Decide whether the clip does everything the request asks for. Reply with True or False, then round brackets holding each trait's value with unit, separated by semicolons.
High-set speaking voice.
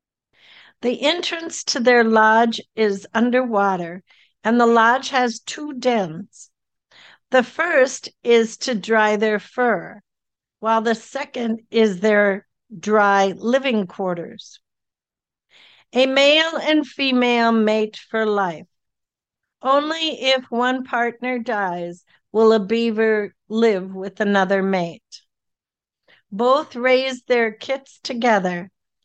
True (230 Hz)